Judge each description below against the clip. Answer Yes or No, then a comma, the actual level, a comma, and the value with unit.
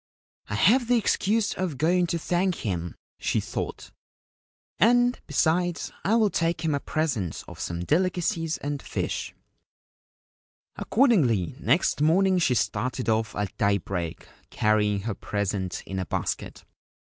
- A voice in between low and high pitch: Yes, medium, 155 Hz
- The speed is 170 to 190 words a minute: No, average, 140 wpm